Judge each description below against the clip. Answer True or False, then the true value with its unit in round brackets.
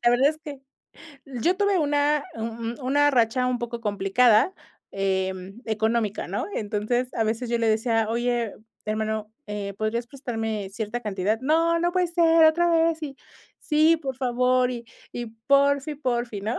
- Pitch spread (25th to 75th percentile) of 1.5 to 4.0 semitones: False (4.8 semitones)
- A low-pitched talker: False (240 Hz)